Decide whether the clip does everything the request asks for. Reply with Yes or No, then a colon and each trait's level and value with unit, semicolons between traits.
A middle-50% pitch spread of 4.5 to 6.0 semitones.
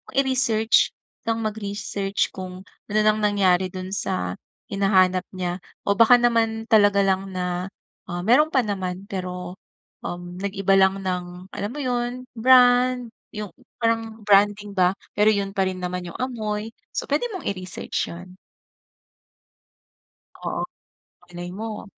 No: average, 3.4 semitones